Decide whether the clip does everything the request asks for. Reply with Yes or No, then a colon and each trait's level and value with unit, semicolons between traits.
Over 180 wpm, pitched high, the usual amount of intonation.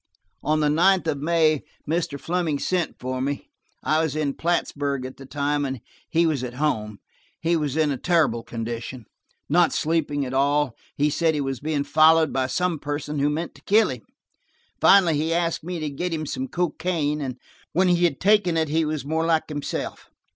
No: average, 195 wpm; medium, 155 Hz; average, 3.0 semitones